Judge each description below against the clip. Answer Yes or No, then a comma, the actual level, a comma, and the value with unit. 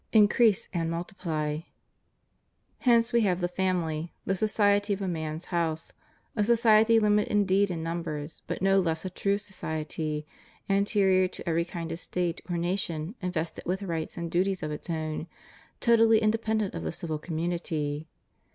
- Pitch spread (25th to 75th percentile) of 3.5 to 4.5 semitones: Yes, average, 3.9 semitones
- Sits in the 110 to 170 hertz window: No, medium, 180 Hz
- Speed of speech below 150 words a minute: No, average, 160 wpm